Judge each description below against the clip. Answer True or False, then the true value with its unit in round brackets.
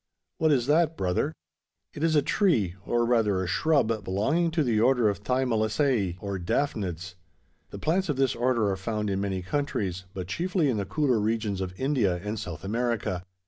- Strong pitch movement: True (6.3 semitones)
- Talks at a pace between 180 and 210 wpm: True (185 wpm)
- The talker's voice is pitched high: False (110 Hz)